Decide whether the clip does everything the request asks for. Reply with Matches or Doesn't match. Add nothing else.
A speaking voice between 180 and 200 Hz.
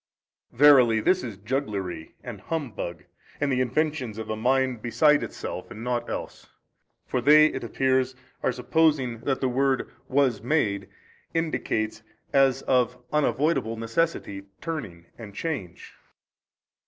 Doesn't match